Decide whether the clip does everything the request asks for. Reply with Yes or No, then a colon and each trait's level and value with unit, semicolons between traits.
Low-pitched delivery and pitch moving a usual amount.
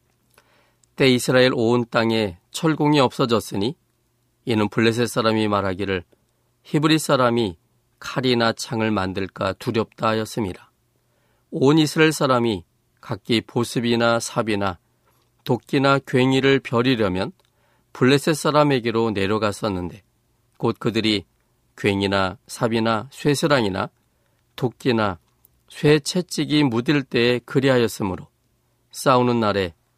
Yes: low, 120 Hz; average, 3.8 semitones